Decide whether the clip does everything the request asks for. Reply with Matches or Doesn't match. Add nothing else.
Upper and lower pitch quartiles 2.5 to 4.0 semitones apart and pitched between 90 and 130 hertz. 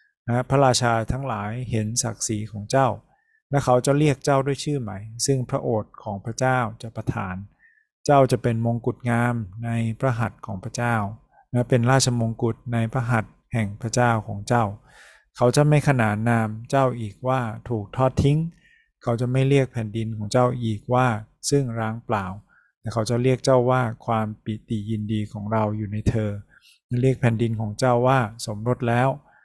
Matches